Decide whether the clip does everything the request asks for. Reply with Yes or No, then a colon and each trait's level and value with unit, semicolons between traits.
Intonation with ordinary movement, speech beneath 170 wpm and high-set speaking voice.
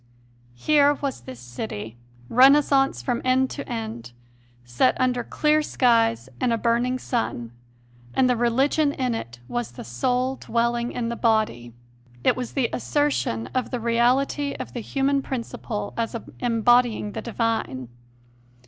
Yes: average, 3.6 semitones; average, 145 wpm; high, 235 Hz